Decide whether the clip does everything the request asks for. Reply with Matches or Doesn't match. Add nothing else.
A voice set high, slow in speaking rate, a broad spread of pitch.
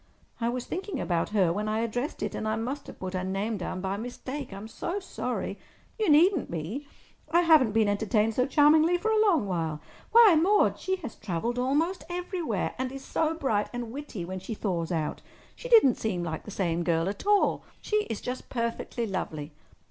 Doesn't match